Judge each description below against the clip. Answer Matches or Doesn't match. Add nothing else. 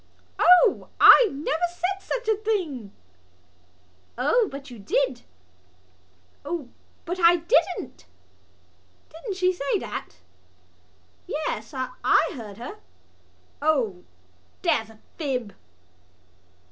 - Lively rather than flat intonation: Matches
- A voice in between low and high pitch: Doesn't match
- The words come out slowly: Matches